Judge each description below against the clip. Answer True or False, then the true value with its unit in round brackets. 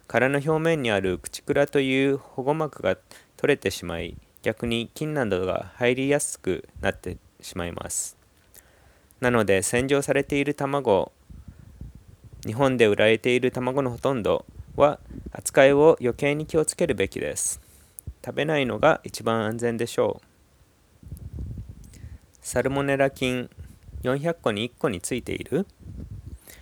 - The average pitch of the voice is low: True (120 Hz)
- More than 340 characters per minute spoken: False (255 characters per minute)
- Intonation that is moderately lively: False (5.8 semitones)